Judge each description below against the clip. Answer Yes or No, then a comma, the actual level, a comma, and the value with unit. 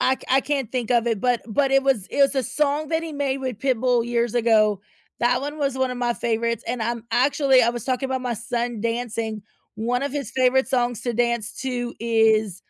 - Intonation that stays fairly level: Yes, narrow, 2.3 semitones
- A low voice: No, high, 245 Hz